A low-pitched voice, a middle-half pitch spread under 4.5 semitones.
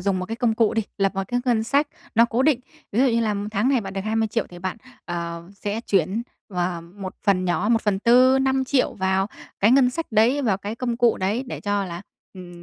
No: high, 215 Hz; average, 4.1 semitones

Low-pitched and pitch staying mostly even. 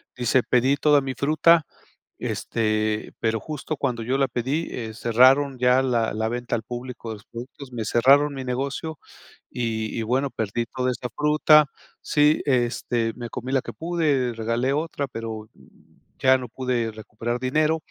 No: low, 125 Hz; average, 3.3 semitones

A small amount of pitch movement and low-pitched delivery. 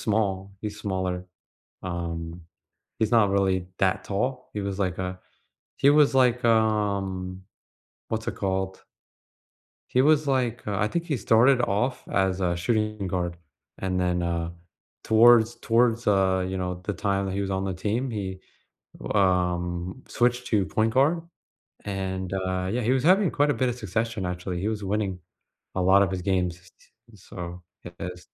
No: average, 3.6 semitones; low, 100 Hz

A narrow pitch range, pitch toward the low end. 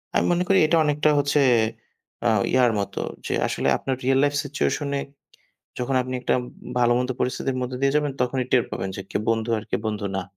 No: average, 3.0 semitones; low, 130 Hz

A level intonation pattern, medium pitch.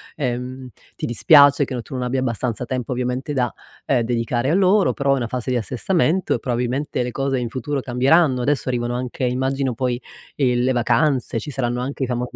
No: narrow, 2.0 semitones; low, 125 Hz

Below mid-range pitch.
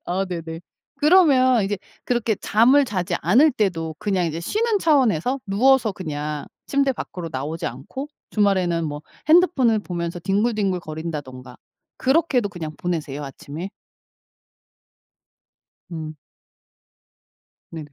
No: high, 190 Hz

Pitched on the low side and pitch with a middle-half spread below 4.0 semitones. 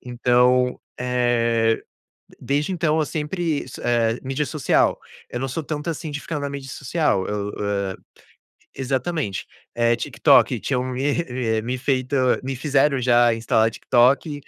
Yes: low, 130 Hz; average, 3.4 semitones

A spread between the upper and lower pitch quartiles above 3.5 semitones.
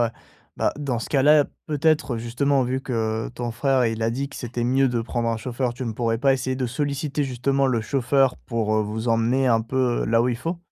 No: average, 2.9 semitones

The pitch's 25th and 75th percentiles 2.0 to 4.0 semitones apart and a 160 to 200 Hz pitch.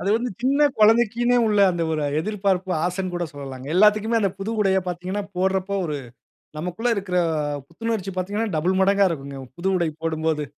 Yes: average, 3.5 semitones; high, 190 Hz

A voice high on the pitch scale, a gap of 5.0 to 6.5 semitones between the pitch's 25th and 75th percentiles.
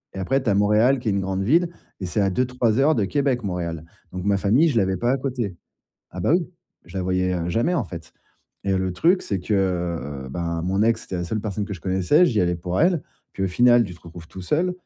No: low, 100 Hz; wide, 5.4 semitones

